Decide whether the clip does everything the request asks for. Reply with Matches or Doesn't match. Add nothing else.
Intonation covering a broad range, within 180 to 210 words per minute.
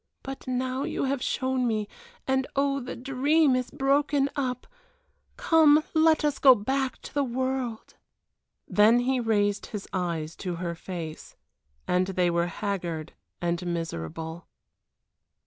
Doesn't match